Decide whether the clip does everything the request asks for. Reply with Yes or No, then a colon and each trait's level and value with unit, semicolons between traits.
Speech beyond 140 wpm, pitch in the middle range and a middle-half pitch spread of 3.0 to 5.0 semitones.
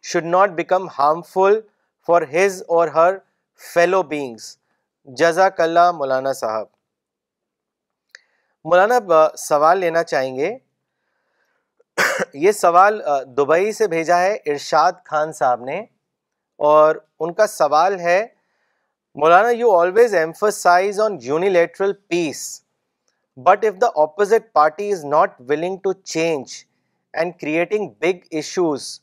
No: average, 115 wpm; medium, 175 Hz; average, 4.5 semitones